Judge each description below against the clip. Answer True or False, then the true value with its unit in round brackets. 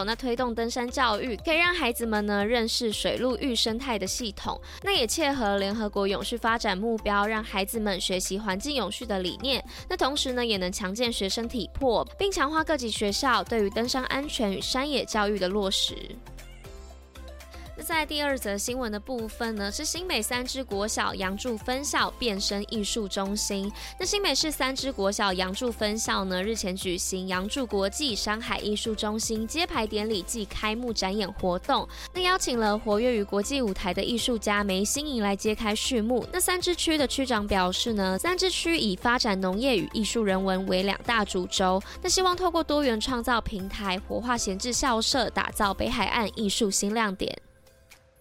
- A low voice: False (225 Hz)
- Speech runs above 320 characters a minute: False (280 characters per minute)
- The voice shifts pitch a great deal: False (4.2 semitones)